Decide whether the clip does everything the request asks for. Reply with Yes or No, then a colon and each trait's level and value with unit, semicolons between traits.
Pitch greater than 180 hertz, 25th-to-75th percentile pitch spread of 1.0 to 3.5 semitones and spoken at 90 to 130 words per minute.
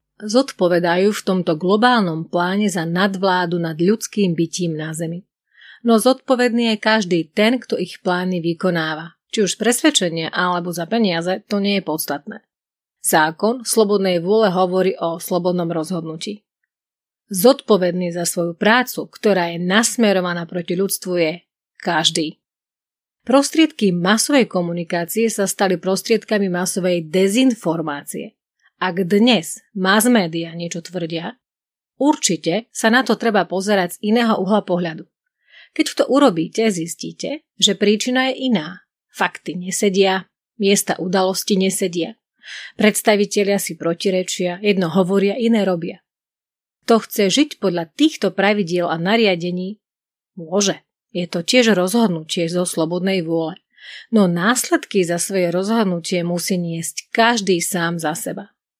No: high, 190 Hz; average, 4.0 semitones; average, 120 wpm